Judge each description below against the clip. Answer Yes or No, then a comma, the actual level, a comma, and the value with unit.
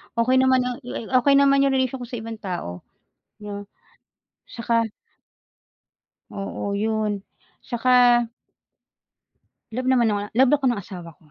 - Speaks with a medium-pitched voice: No, high, 235 Hz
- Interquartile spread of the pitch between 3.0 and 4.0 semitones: Yes, average, 3.6 semitones